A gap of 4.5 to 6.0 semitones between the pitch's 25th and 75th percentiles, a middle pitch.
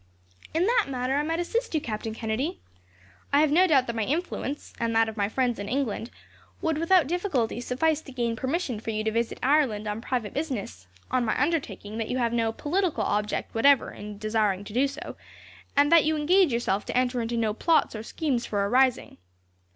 No: wide, 5.5 semitones; very high, 250 Hz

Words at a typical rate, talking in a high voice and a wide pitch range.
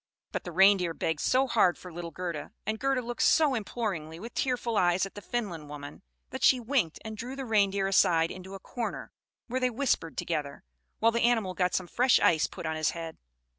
No: fast, 210 wpm; high, 195 Hz; wide, 6.2 semitones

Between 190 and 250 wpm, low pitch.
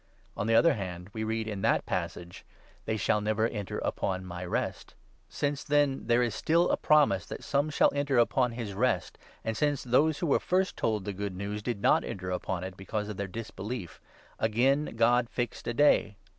Yes: fast, 205 wpm; low, 110 Hz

